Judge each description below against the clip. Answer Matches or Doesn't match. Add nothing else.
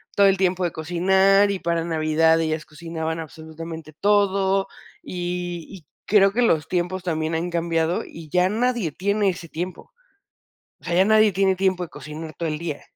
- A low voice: Doesn't match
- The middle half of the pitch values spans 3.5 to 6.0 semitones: Doesn't match